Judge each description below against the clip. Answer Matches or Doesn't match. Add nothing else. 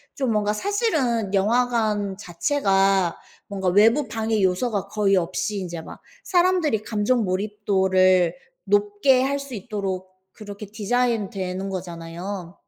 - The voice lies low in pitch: Doesn't match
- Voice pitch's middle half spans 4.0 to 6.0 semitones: Doesn't match